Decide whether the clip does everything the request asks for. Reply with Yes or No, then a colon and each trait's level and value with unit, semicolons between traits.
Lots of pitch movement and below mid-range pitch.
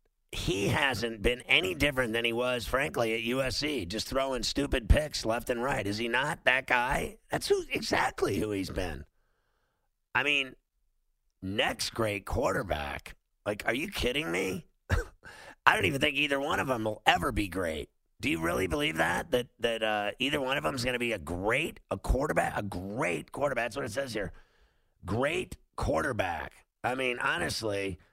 No: average, 4.2 semitones; low, 120 Hz